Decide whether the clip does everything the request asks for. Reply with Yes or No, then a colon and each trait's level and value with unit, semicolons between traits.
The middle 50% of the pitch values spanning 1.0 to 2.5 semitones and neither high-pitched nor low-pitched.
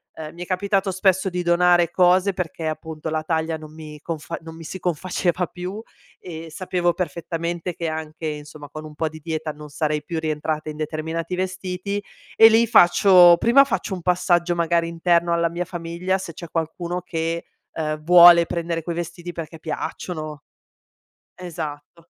Yes: narrow, 2.1 semitones; medium, 170 Hz